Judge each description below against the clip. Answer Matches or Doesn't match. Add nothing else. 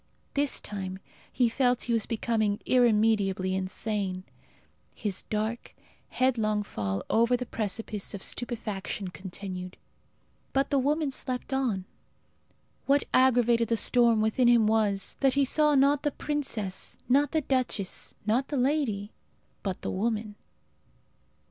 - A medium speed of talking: Doesn't match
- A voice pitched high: Matches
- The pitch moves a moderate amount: Matches